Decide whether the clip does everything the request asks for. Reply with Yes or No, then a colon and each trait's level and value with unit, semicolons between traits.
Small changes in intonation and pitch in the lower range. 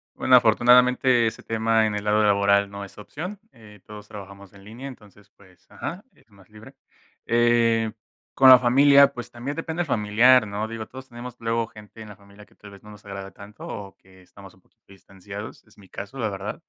No: average, 3.2 semitones; low, 110 Hz